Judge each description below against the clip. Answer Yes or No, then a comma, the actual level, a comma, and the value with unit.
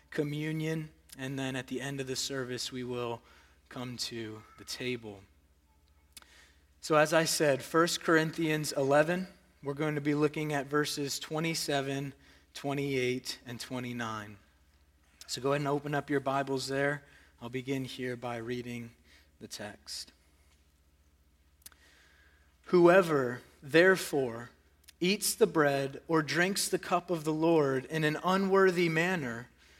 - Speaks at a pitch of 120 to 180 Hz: Yes, low, 135 Hz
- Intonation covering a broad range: Yes, wide, 6.3 semitones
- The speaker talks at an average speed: No, slow, 130 wpm